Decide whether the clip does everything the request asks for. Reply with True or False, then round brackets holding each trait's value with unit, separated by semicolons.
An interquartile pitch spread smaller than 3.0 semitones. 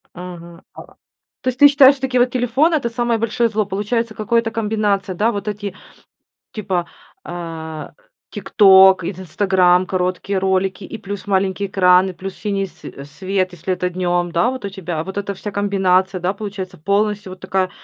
True (2.6 semitones)